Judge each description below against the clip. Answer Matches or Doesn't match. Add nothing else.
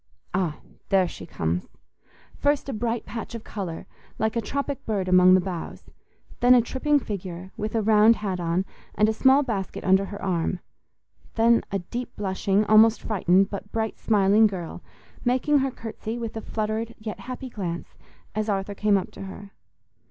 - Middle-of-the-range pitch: Doesn't match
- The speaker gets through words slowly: Doesn't match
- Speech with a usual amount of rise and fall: Matches